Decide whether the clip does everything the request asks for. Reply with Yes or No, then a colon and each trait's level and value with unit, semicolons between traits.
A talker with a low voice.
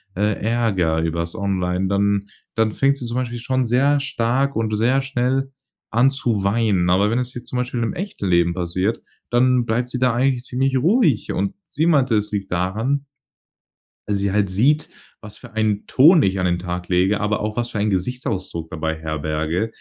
Yes: low, 110 Hz